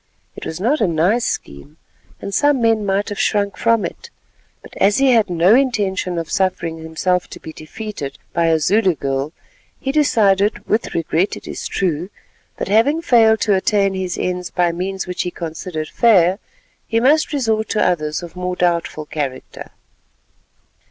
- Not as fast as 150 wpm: No, average, 165 wpm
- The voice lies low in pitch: No, high, 190 Hz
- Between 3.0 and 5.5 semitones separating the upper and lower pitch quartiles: Yes, average, 4.7 semitones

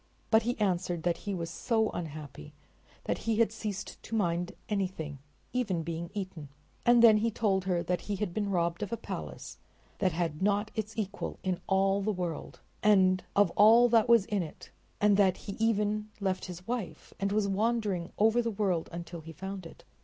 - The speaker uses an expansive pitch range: No, average, 3.5 semitones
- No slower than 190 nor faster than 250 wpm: Yes, average, 195 wpm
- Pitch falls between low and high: No, high, 195 Hz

